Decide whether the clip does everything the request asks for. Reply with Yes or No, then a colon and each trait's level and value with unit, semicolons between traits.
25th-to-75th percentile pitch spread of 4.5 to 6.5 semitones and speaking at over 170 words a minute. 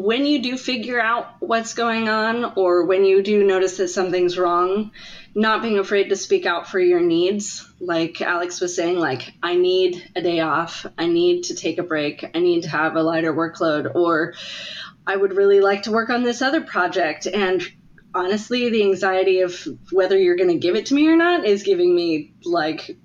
Yes: average, 4.8 semitones; fast, 205 wpm